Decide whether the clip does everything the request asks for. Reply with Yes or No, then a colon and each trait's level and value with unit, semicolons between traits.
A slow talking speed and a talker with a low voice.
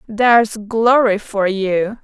No: slow, 120 wpm; high, 215 Hz